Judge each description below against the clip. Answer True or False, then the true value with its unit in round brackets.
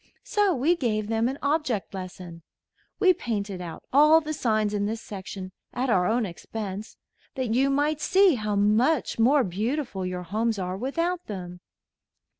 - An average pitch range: False (6.3 semitones)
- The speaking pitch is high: True (225 Hz)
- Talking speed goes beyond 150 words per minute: True (160 wpm)